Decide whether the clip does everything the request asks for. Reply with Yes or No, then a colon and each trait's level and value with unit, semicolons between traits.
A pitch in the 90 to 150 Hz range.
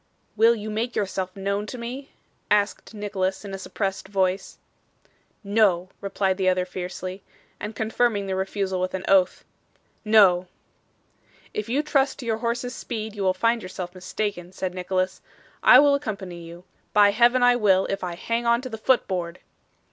No: high, 200 Hz